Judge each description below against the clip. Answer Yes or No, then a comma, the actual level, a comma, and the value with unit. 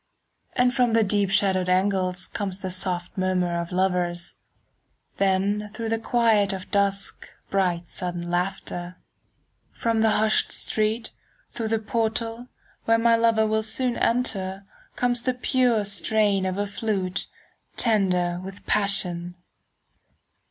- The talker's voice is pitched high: Yes, high, 200 Hz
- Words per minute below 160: Yes, slow, 135 wpm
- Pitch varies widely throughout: No, average, 3.4 semitones